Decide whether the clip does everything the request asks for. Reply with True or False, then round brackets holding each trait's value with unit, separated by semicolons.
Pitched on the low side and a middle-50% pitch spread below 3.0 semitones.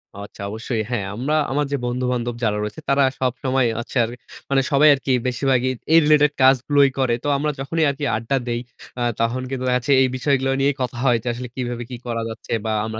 True (130 Hz; 2.6 semitones)